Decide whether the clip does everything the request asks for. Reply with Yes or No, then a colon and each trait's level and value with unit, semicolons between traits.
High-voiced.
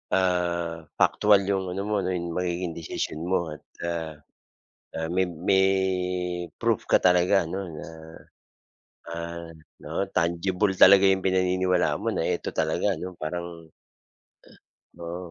No: very low, 90 Hz